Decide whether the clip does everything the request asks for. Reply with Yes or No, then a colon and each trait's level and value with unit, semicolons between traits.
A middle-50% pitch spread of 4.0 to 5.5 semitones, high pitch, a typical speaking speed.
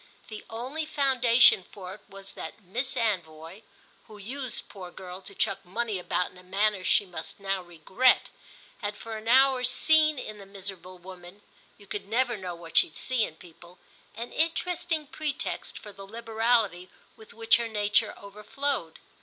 Yes: average, 4.6 semitones; high, 210 Hz; average, 160 wpm